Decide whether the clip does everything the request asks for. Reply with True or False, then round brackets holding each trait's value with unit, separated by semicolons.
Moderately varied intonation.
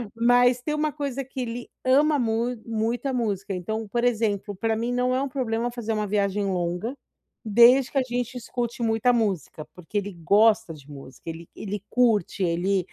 True (3.7 semitones)